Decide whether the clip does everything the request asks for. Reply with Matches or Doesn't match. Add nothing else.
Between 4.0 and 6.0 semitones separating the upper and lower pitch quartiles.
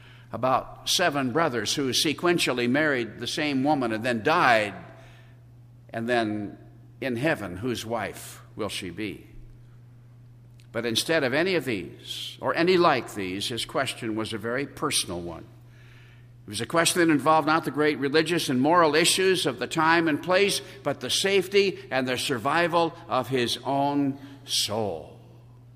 Matches